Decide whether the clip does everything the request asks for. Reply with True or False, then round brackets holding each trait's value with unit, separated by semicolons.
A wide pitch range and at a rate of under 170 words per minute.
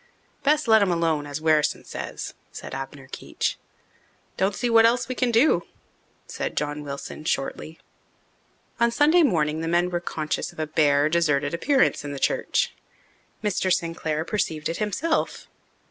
True (6.9 semitones; 155 wpm)